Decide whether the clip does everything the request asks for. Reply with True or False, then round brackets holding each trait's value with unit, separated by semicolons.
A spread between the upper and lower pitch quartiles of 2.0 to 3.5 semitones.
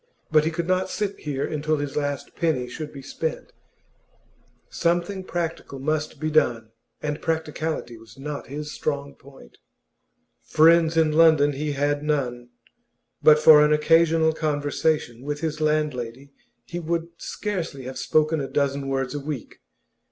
True (2.4 semitones)